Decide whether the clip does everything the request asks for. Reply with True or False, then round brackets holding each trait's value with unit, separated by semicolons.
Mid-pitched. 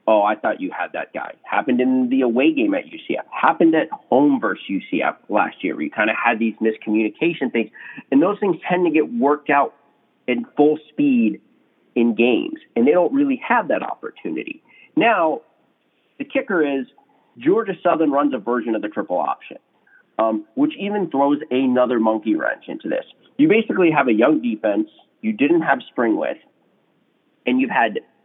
True (180 Hz)